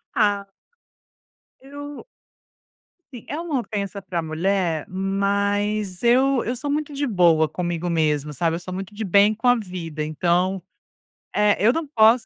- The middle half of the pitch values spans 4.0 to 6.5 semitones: Yes, average, 5.3 semitones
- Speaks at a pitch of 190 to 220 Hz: Yes, high, 200 Hz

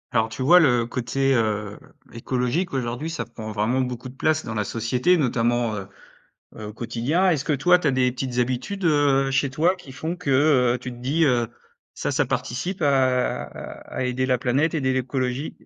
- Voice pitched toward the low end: Yes, low, 130 Hz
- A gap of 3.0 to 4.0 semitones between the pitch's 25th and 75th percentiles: Yes, average, 3.4 semitones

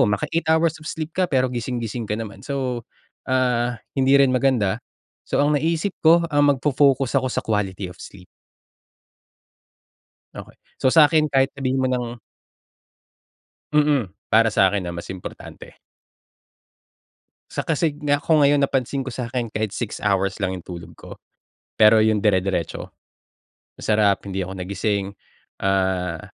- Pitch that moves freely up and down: Yes, wide, 5.9 semitones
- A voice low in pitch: Yes, low, 120 Hz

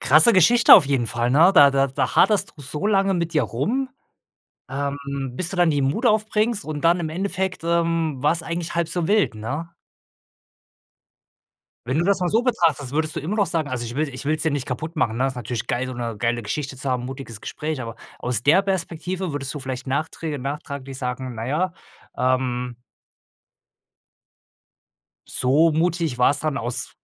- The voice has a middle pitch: Yes, medium, 150 Hz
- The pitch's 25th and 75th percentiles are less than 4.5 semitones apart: No, average, 4.8 semitones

